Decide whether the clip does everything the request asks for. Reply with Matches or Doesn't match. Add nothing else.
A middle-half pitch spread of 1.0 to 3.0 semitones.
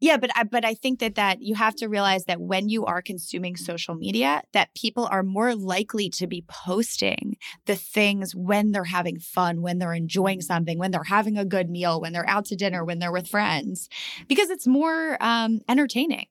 Doesn't match